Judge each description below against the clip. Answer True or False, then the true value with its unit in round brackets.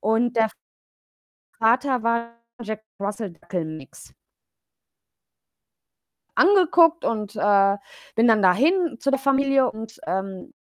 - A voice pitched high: True (225 Hz)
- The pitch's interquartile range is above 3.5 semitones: True (5.0 semitones)